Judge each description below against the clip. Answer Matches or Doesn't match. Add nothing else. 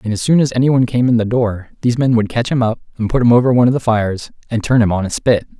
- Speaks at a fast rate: Matches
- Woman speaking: Doesn't match